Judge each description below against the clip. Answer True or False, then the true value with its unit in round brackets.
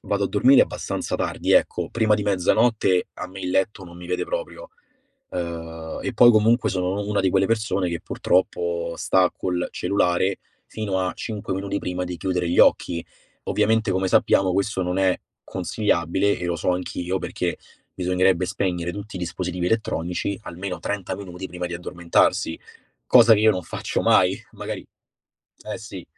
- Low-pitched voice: True (95 Hz)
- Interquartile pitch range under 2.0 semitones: False (2.5 semitones)